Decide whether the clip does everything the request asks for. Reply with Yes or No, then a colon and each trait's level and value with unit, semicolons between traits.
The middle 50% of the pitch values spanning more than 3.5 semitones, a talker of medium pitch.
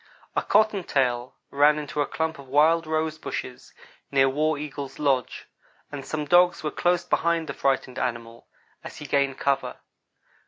No: average, 2.8 semitones; medium, 145 Hz